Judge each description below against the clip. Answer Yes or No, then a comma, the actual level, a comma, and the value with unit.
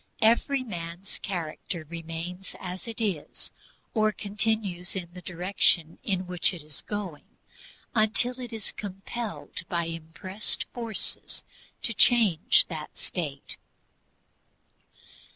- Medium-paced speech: No, slow, 110 wpm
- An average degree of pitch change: Yes, average, 4.3 semitones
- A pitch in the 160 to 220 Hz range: Yes, medium, 185 Hz